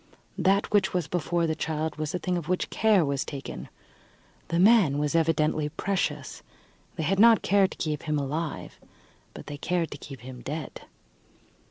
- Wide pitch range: No, average, 3.5 semitones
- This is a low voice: No, medium, 160 Hz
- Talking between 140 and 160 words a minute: No, average, 175 wpm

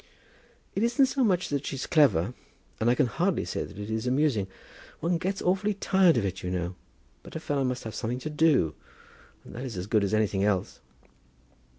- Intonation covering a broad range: Yes, wide, 8.2 semitones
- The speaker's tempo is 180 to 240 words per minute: Yes, fast, 205 wpm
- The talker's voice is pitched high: No, low, 125 Hz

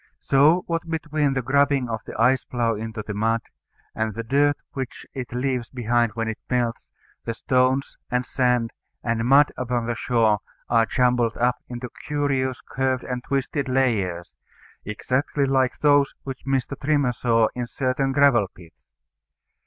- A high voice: No, low, 125 Hz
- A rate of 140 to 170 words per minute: Yes, average, 155 wpm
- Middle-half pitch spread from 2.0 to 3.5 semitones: Yes, average, 2.8 semitones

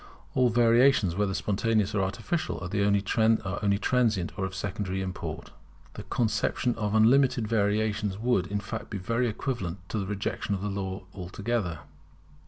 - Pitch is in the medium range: No, low, 105 Hz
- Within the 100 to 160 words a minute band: Yes, average, 140 wpm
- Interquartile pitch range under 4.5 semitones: Yes, average, 2.9 semitones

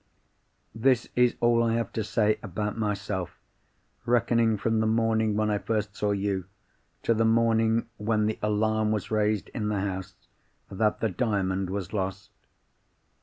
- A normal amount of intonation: No, narrow, 1.9 semitones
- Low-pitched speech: Yes, low, 110 Hz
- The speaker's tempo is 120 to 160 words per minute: Yes, average, 155 wpm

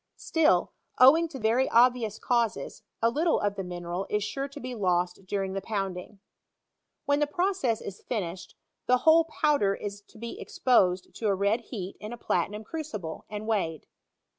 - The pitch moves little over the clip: No, average, 4.8 semitones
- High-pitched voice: Yes, high, 215 Hz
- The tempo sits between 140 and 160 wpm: No, average, 170 wpm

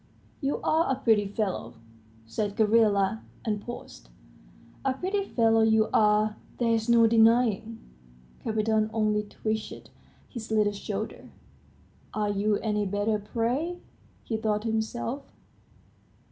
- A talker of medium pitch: No, high, 220 Hz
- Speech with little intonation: Yes, narrow, 1.6 semitones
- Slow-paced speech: Yes, slow, 115 wpm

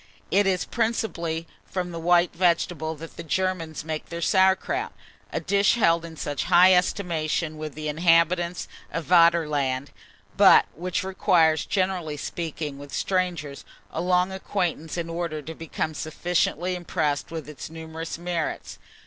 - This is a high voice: No, medium, 170 Hz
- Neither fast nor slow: Yes, average, 145 wpm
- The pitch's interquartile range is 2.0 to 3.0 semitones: Yes, narrow, 2.4 semitones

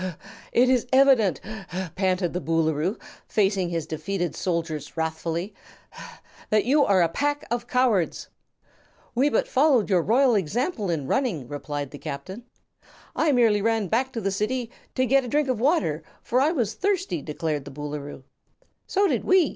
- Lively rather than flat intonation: Yes, wide, 7.8 semitones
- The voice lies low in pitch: No, high, 205 Hz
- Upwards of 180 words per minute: No, average, 165 wpm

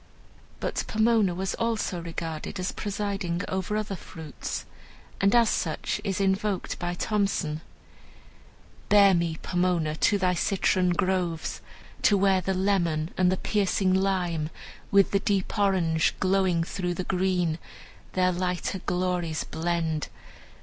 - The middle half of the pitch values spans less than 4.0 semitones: Yes, narrow, 2.4 semitones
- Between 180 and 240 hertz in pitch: Yes, medium, 185 Hz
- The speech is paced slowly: Yes, slow, 130 wpm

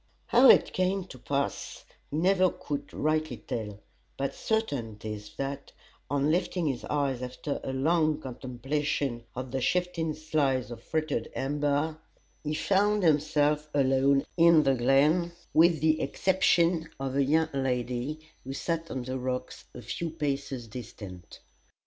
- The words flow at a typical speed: Yes, average, 145 wpm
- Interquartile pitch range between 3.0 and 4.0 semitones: Yes, average, 3.7 semitones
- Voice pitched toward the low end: No, medium, 145 Hz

